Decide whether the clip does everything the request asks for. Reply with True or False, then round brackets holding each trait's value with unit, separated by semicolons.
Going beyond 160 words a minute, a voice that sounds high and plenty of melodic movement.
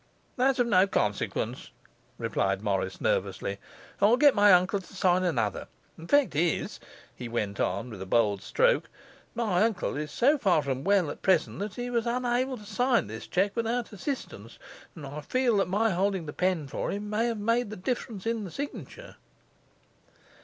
True (180 wpm; 200 Hz; 6.4 semitones)